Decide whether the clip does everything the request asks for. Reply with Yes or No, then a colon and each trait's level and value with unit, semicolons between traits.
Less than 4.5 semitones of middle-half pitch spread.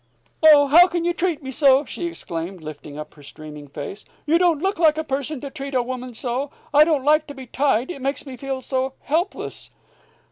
Yes: average, 4.0 semitones